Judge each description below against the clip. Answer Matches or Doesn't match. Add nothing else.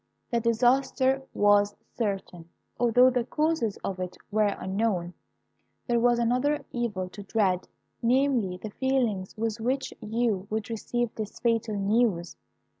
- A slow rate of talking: Matches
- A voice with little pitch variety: Doesn't match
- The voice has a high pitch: Matches